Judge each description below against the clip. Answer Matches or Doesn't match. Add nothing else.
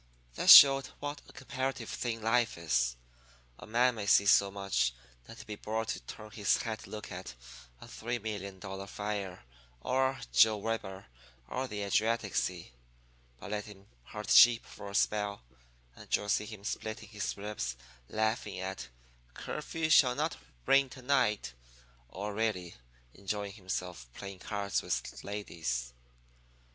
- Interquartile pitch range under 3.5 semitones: Matches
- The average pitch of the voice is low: Matches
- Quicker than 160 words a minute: Doesn't match